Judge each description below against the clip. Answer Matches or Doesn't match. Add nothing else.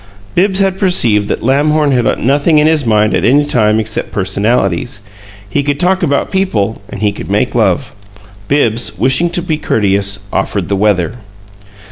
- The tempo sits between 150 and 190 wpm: Matches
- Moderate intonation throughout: Doesn't match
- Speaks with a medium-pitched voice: Doesn't match